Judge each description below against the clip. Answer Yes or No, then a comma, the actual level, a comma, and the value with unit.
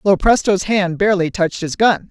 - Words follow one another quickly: No, average, 170 wpm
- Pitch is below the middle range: No, high, 190 Hz